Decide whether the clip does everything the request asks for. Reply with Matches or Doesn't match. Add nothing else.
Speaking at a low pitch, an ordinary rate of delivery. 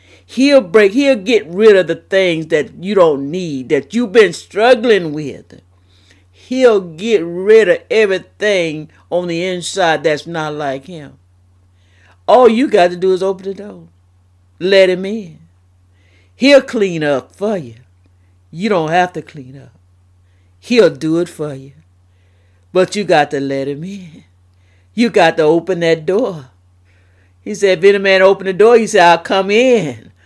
Doesn't match